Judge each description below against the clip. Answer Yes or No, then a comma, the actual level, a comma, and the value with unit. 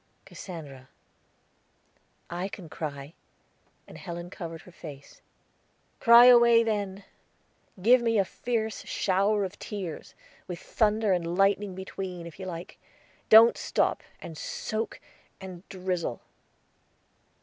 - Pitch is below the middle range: No, high, 190 Hz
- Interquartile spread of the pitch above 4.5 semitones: No, average, 4.0 semitones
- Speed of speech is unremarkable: No, slow, 115 wpm